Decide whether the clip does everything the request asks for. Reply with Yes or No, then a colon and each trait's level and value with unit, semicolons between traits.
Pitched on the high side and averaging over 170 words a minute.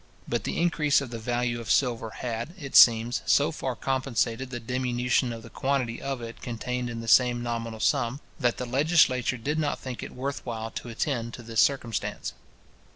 No: low, 120 Hz; average, 190 wpm